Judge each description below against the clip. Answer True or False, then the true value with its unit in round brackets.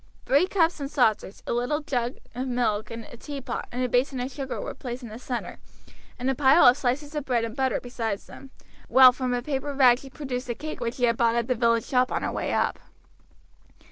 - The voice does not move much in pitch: True (2.2 semitones)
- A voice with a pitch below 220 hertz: False (250 Hz)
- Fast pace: True (225 wpm)